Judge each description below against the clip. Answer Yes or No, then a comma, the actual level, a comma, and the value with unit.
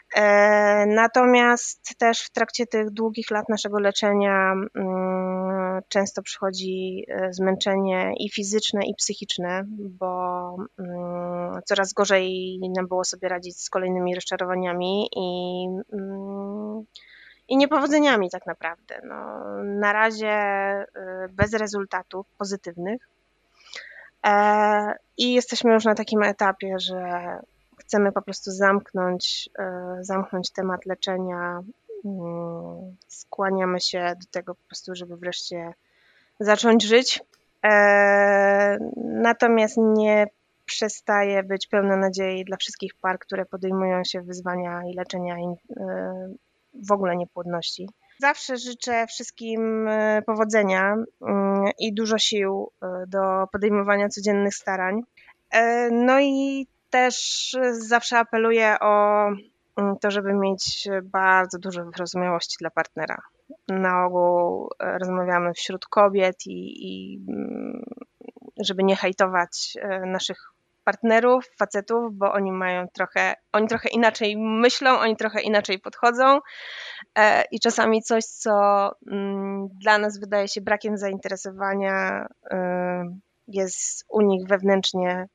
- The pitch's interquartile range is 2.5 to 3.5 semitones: Yes, average, 2.8 semitones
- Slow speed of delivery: Yes, slow, 100 wpm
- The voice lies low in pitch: No, high, 200 Hz